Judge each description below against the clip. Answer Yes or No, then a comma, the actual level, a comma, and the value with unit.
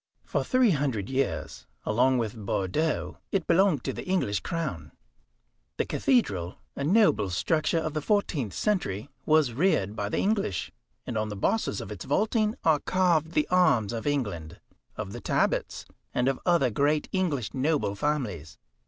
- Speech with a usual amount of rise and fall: No, wide, 8.7 semitones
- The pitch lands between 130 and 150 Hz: Yes, medium, 140 Hz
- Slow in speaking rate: No, average, 160 wpm